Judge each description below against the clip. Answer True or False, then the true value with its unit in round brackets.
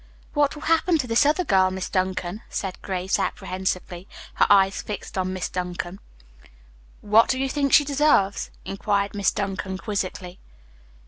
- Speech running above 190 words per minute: False (150 wpm)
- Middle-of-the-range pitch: False (195 Hz)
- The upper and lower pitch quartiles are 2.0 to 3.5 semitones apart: False (5.5 semitones)